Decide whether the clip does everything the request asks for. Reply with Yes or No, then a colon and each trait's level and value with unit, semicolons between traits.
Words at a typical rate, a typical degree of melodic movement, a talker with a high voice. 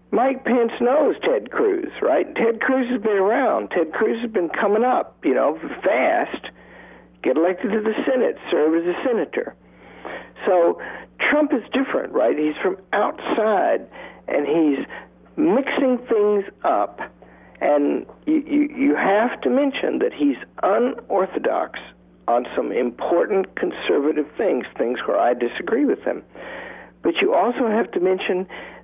No: average, 145 wpm; wide, 6.6 semitones; high, 235 Hz